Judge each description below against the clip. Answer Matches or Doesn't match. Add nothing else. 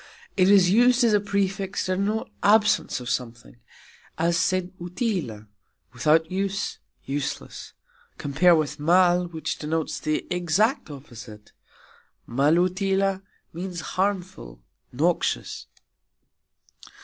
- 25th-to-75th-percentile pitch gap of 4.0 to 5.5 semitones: Matches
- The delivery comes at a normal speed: Doesn't match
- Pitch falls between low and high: Matches